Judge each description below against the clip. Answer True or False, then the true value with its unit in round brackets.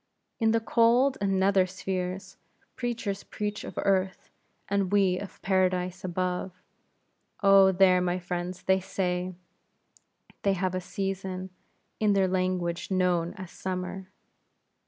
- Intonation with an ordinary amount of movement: False (1.3 semitones)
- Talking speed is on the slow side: True (125 wpm)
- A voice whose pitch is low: False (185 Hz)